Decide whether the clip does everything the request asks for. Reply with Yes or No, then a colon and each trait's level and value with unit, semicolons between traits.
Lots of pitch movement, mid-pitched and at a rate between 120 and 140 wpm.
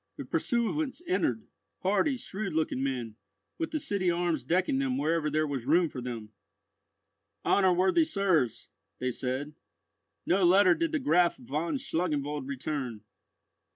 Yes: wide, 6.6 semitones; medium, 165 Hz; slow, 135 wpm